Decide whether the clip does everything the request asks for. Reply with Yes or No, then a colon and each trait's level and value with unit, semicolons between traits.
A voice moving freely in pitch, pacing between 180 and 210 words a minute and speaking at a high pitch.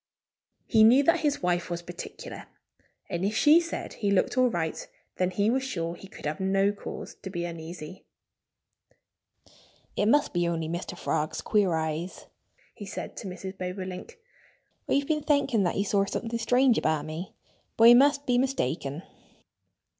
No: wide, 6.1 semitones; average, 165 wpm; high, 195 Hz